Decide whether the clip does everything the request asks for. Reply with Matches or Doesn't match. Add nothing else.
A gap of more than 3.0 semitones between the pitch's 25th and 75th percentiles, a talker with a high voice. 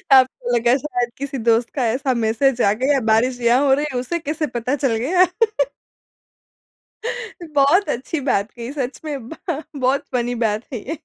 Matches